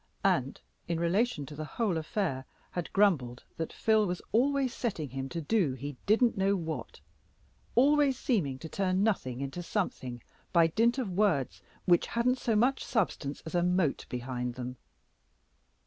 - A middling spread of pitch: No, wide, 7.8 semitones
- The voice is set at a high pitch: No, medium, 175 Hz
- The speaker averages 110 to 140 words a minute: No, average, 160 wpm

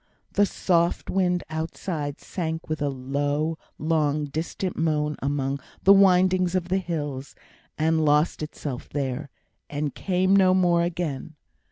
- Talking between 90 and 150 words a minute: Yes, slow, 135 wpm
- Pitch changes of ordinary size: Yes, average, 3.6 semitones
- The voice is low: No, medium, 160 Hz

